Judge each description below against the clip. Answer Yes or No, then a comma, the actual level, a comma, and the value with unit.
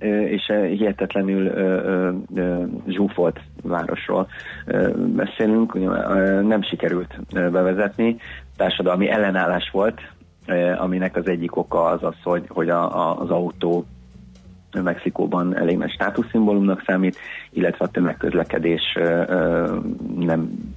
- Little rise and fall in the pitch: Yes, narrow, 2.3 semitones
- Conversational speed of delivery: No, slow, 85 wpm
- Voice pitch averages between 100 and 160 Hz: No, very low, 90 Hz